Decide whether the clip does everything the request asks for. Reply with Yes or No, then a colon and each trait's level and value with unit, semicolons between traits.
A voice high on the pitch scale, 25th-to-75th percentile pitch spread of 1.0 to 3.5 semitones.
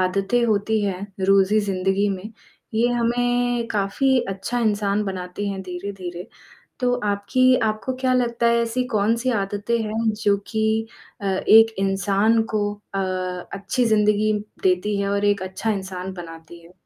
Yes: high, 205 Hz; average, 2.9 semitones